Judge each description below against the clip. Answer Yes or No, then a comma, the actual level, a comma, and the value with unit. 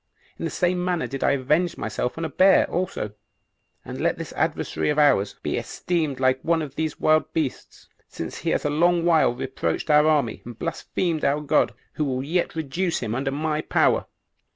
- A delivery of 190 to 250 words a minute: Yes, average, 195 wpm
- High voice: No, medium, 150 Hz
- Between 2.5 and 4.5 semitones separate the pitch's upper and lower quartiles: Yes, average, 3.8 semitones